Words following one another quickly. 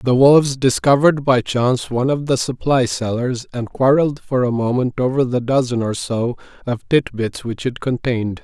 No: average, 185 wpm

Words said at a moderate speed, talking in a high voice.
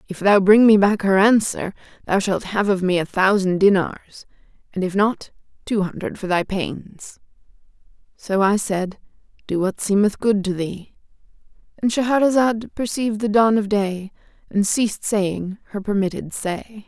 Yes: average, 155 wpm; high, 200 Hz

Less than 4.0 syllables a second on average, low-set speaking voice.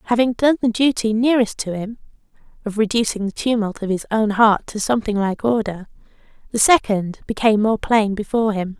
No: 3.6 syllables/s; high, 220 Hz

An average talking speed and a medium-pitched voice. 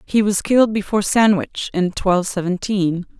No: average, 150 wpm; high, 195 Hz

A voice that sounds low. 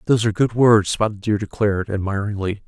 Yes: low, 105 Hz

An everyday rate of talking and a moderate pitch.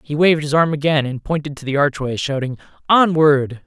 Yes: average, 195 wpm; medium, 145 Hz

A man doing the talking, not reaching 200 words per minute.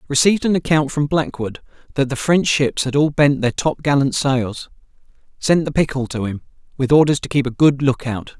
No: male; fast, 205 wpm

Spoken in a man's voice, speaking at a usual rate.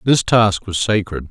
Yes: male; average, 185 wpm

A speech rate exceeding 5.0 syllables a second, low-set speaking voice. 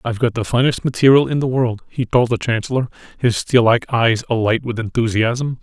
Yes: 5.5 syllables/s; low, 120 Hz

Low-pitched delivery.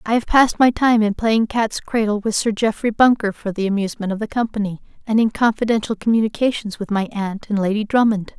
No: high, 215 Hz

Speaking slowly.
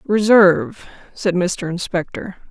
Yes: slow, 95 wpm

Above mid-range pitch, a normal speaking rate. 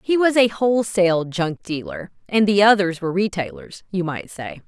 Yes: high, 195 Hz; average, 180 wpm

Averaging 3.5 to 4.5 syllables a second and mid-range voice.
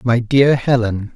No: 3.8 syllables/s; low, 120 Hz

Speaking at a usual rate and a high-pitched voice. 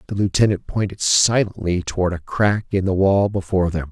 No: average, 185 wpm; very low, 95 Hz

